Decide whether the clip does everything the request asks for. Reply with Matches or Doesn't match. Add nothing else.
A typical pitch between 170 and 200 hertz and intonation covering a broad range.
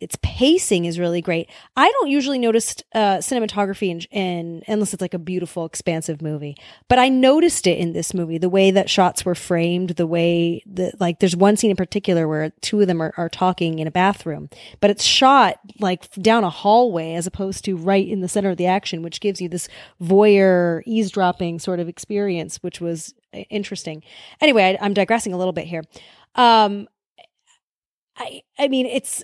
Doesn't match